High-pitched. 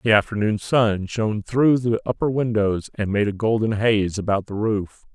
No: low, 110 Hz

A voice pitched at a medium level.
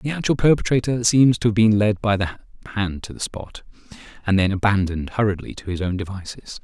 No: low, 105 Hz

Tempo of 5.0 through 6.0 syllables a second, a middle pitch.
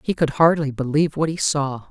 Yes: 5.6 syllables/s; medium, 145 Hz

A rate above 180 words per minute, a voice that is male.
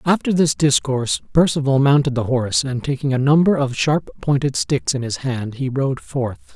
Yes: average, 190 wpm; male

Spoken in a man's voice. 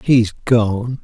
Yes: male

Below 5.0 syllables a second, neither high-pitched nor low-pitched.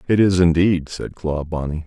No: 4.8 syllables/s; very low, 85 Hz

